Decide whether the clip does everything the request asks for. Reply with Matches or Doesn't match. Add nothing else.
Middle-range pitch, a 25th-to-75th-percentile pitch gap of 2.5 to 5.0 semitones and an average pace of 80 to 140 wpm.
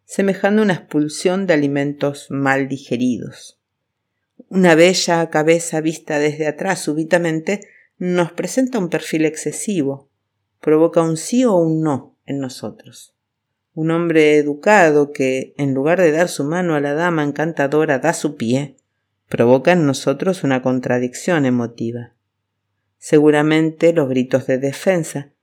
Matches